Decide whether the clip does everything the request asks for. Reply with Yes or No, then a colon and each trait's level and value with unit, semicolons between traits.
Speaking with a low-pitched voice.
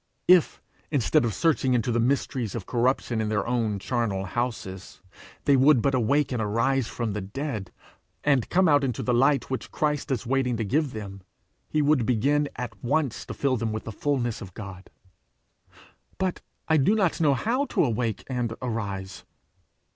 Yes: low, 125 Hz